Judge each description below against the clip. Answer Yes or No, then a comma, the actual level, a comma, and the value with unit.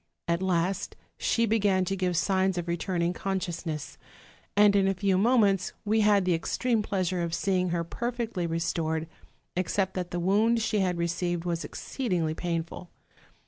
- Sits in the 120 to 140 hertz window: No, medium, 185 Hz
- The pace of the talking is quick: No, average, 170 wpm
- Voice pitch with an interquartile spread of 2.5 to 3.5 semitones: Yes, average, 2.8 semitones